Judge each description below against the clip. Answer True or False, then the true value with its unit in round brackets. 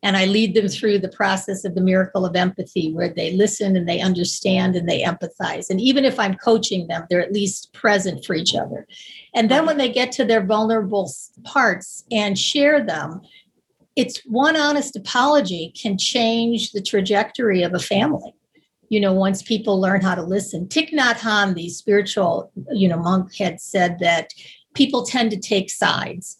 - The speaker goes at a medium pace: True (185 wpm)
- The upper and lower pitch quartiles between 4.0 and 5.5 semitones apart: False (3.4 semitones)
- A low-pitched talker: False (200 Hz)